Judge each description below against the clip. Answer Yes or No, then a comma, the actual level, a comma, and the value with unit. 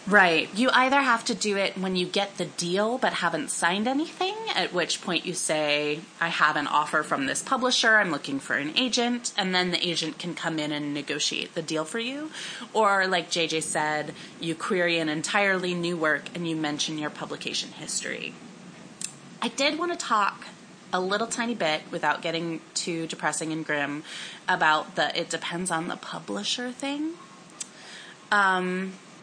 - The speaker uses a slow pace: No, average, 175 wpm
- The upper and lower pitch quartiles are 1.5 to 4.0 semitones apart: No, average, 5.3 semitones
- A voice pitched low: No, medium, 175 Hz